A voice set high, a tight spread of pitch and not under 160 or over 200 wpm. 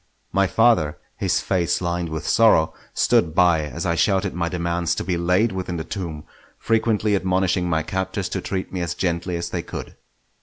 No: very low, 90 Hz; narrow, 2.1 semitones; average, 185 wpm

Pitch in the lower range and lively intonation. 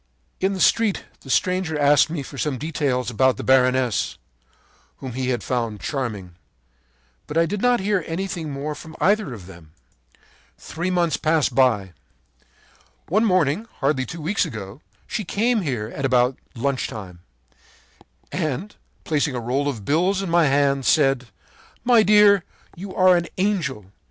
No: medium, 145 Hz; wide, 6.3 semitones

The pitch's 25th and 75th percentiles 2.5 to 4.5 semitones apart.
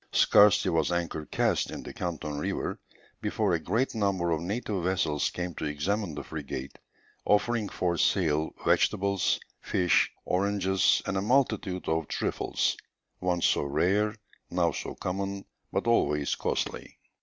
Yes: average, 3.9 semitones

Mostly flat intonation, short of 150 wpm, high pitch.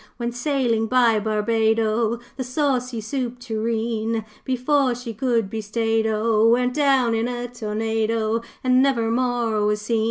Yes: narrow, 2.0 semitones; average, 140 wpm; high, 230 Hz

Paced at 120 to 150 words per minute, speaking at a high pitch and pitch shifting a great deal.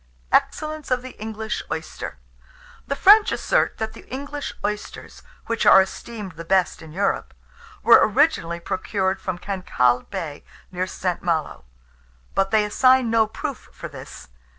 Yes: average, 145 wpm; high, 210 Hz; wide, 5.7 semitones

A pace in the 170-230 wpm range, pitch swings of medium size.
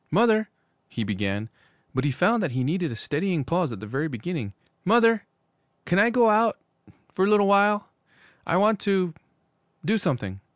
No: average, 175 wpm; wide, 8.4 semitones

